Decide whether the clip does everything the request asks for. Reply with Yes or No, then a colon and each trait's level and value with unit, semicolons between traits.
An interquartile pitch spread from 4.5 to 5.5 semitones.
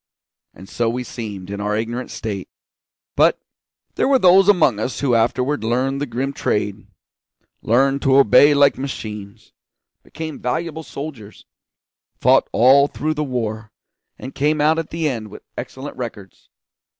Yes: average, 4.9 semitones